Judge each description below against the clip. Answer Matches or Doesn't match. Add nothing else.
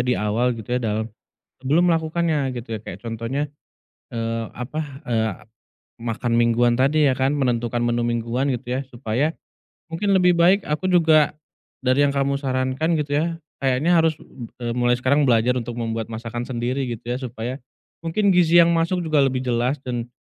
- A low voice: Matches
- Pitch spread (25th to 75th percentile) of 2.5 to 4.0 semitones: Doesn't match